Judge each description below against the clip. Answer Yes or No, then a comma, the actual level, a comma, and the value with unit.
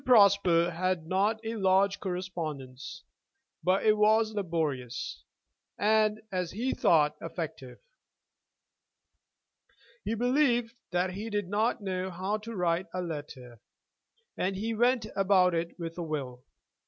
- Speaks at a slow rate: Yes, slow, 120 wpm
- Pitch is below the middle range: No, medium, 185 Hz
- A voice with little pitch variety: No, average, 4.2 semitones